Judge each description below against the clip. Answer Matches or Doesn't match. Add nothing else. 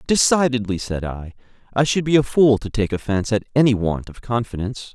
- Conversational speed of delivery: Matches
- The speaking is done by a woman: Doesn't match